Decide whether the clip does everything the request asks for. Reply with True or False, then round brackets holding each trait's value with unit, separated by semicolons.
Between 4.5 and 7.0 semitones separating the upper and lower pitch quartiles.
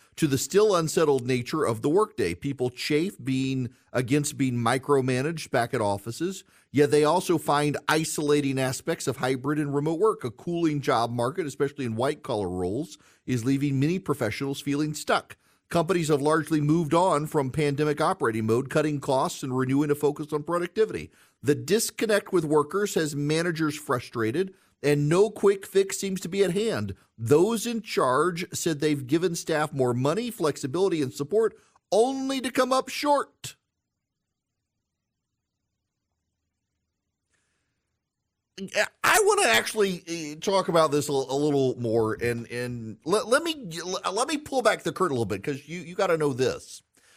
True (5.4 semitones)